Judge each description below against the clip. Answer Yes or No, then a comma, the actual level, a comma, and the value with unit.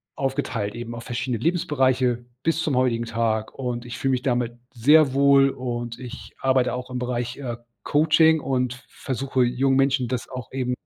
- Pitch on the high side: No, low, 125 Hz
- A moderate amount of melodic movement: No, narrow, 2.1 semitones